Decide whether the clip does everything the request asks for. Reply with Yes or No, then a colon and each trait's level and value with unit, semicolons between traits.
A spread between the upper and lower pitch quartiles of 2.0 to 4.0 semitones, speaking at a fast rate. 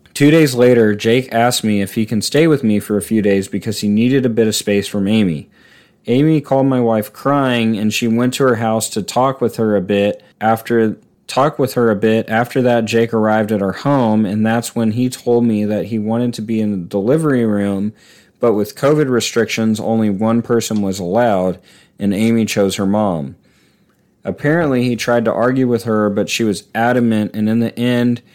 Yes: narrow, 2.4 semitones; fast, 210 wpm